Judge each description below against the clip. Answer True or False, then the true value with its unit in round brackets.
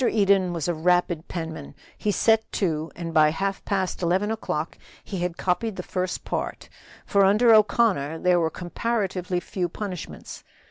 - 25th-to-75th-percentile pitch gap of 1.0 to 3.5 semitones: True (3.1 semitones)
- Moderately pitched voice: True (180 Hz)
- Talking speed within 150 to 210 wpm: True (155 wpm)